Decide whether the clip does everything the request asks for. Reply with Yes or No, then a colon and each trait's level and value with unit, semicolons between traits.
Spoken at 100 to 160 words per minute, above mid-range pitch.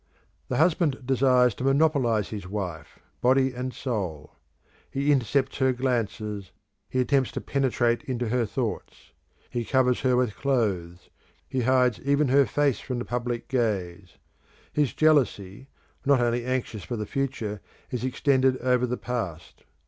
No: average, 145 wpm; low, 125 Hz